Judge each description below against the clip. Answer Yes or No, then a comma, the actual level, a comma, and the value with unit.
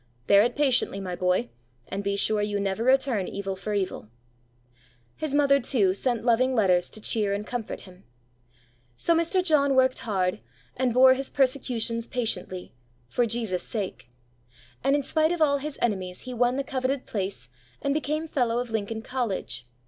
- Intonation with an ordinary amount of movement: Yes, average, 5.0 semitones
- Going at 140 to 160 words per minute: No, average, 170 wpm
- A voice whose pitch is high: Yes, high, 235 Hz